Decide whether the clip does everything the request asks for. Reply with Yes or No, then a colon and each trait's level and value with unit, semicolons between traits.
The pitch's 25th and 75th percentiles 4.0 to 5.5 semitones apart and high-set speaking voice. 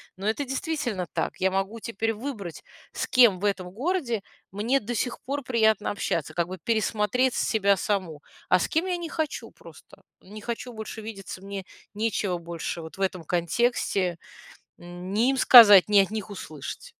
Yes: average, 4.3 semitones; high, 210 Hz